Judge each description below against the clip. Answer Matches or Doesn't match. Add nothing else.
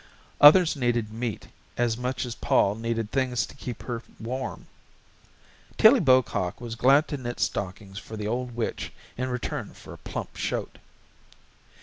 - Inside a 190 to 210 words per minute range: Doesn't match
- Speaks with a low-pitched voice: Matches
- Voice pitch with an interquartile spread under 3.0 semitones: Matches